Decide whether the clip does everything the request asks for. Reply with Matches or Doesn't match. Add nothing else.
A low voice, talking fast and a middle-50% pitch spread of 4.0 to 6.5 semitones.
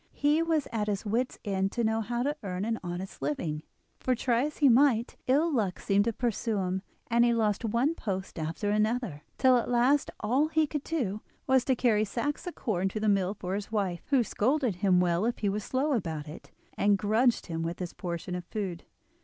Doesn't match